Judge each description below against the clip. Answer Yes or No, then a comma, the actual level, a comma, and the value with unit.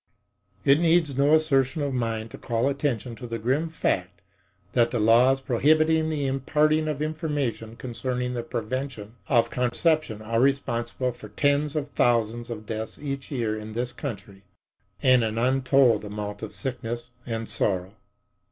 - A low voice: Yes, low, 125 Hz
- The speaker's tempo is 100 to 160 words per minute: Yes, average, 150 wpm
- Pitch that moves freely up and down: No, average, 3.7 semitones